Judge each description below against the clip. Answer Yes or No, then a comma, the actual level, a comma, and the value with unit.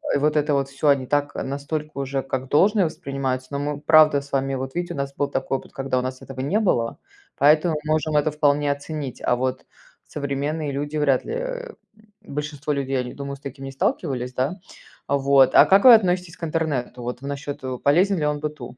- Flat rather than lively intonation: Yes, narrow, 2.3 semitones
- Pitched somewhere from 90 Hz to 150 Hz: Yes, medium, 140 Hz